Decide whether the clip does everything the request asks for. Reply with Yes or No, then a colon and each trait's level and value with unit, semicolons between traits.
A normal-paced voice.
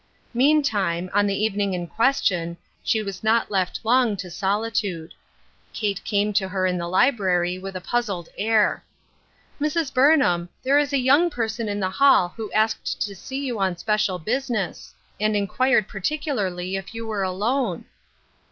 Yes: average, 160 wpm